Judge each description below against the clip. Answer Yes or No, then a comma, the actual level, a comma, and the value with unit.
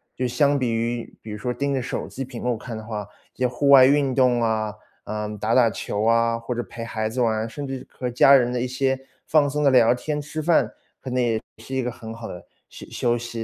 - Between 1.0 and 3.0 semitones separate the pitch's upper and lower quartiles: Yes, average, 2.7 semitones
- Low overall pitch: Yes, low, 120 Hz